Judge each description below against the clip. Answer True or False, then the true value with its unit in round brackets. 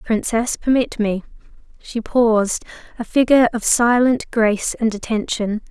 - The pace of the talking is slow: True (125 wpm)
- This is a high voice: True (230 Hz)